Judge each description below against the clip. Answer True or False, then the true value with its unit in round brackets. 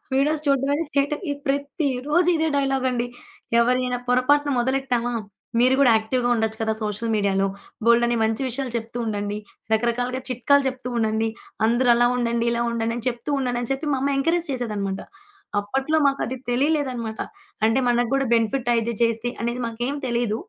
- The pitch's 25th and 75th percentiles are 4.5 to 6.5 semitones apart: False (2.9 semitones)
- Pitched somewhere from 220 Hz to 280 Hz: True (245 Hz)